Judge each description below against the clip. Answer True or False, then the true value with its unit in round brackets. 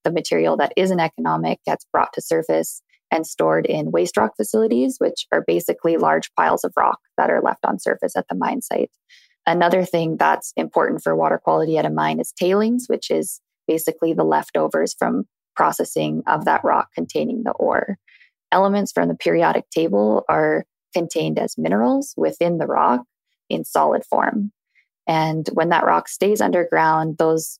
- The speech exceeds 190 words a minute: False (170 wpm)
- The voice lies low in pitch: False (160 Hz)